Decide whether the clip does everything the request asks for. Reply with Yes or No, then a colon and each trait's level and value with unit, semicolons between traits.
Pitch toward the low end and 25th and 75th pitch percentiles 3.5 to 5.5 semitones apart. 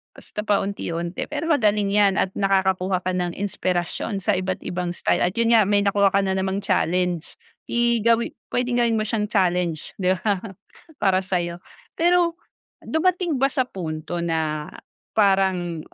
No: high, 195 Hz; average, 3.8 semitones